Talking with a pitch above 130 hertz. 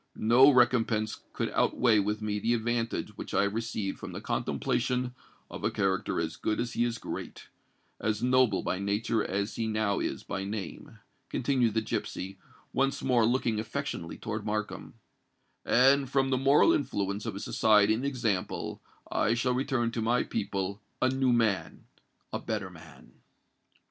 No: low, 115 Hz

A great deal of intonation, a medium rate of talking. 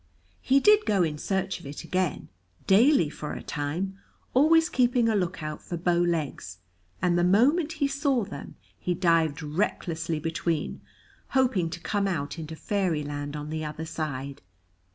Yes: wide, 5.7 semitones; average, 160 wpm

